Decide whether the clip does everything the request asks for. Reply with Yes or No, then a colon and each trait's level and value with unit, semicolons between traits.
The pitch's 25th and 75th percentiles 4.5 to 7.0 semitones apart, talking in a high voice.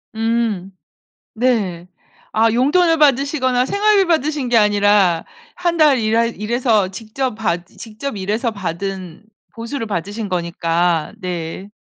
Yes: average, 5.3 semitones; high, 220 Hz